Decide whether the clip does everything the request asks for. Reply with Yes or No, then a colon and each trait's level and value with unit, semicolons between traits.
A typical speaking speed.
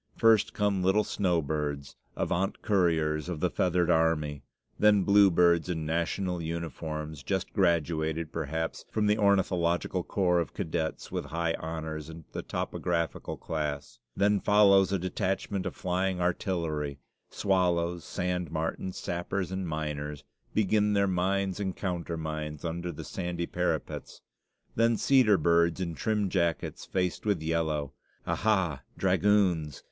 No: slow, 130 wpm